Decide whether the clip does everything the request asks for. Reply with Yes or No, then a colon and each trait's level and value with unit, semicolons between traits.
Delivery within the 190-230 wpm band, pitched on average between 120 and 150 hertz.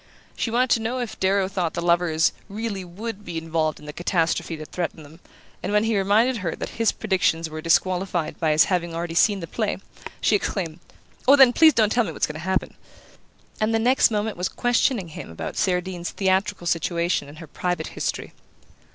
No: average, 200 wpm; medium, 185 Hz